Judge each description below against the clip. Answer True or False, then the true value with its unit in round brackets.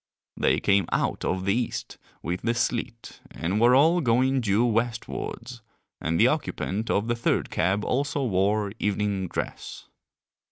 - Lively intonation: False (3.5 semitones)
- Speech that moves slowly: False (150 wpm)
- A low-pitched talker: True (115 Hz)